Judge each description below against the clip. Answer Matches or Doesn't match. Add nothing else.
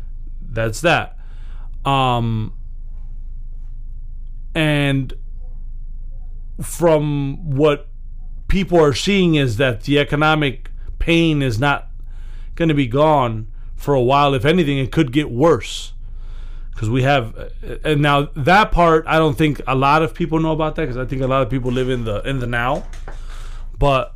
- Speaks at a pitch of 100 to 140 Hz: Matches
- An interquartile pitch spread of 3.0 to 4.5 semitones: Doesn't match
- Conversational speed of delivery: Matches